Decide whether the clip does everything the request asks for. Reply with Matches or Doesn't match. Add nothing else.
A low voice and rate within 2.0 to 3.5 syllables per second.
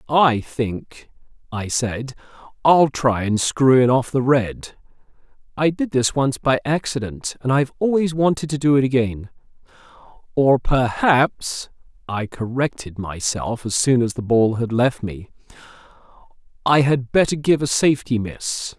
Matches